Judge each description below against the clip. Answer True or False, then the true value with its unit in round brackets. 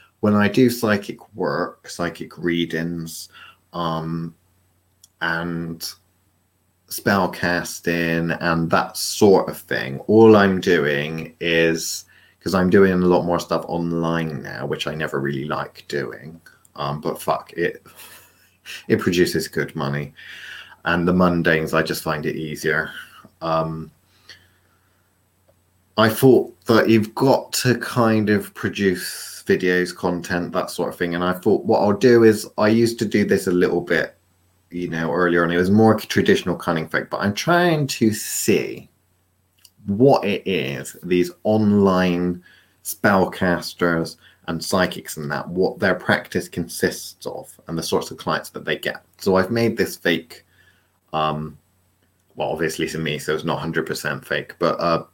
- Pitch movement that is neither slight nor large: True (3.2 semitones)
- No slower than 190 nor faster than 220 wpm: False (150 wpm)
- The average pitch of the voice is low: True (90 Hz)